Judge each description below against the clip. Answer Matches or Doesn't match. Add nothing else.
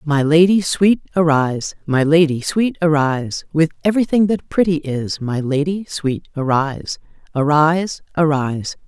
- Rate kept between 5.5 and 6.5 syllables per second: Doesn't match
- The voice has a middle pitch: Matches